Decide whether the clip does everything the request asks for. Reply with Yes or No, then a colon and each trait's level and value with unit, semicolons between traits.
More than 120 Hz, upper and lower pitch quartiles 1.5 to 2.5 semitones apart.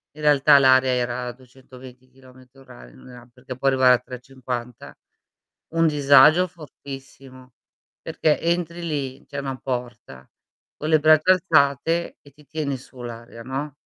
No: low, 135 Hz; average, 2.9 semitones